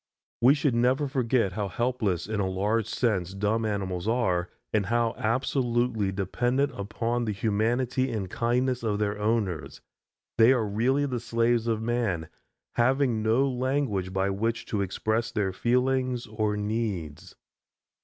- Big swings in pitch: No, average, 3.3 semitones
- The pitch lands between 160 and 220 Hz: No, low, 115 Hz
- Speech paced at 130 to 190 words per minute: Yes, average, 145 wpm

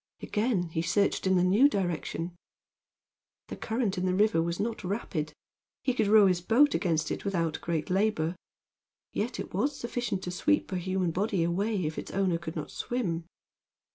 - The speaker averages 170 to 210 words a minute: Yes, average, 175 wpm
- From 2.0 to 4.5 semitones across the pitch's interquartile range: Yes, average, 4.2 semitones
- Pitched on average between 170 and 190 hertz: Yes, medium, 185 Hz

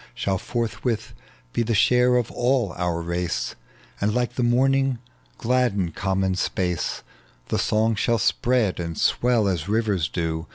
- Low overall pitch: Yes, low, 110 Hz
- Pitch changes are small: No, average, 5.1 semitones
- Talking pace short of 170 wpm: Yes, average, 140 wpm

